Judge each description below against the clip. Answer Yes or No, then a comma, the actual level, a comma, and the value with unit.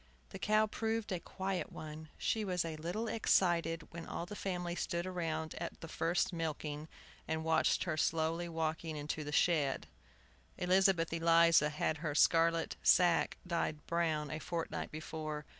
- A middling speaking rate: Yes, average, 155 wpm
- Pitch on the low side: No, medium, 165 Hz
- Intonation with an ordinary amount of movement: No, narrow, 2.0 semitones